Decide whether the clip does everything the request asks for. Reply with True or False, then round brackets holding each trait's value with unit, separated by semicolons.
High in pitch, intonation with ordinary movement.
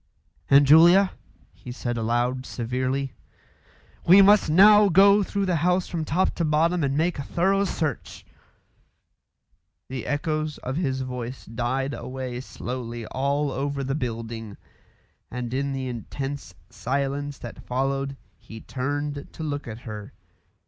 False (140 Hz; 3.9 semitones)